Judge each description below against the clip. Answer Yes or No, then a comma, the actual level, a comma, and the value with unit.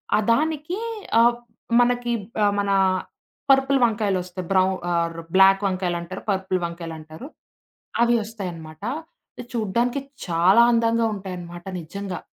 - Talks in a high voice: Yes, high, 195 Hz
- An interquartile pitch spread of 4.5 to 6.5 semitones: Yes, average, 5.1 semitones